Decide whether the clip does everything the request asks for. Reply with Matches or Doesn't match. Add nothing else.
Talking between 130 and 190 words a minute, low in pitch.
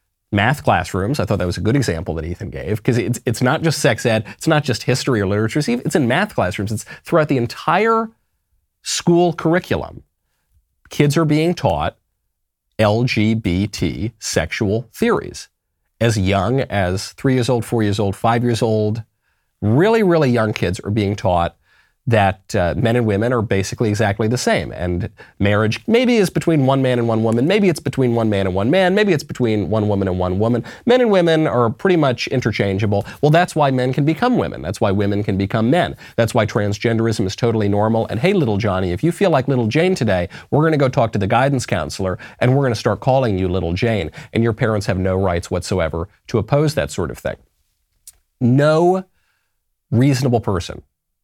Doesn't match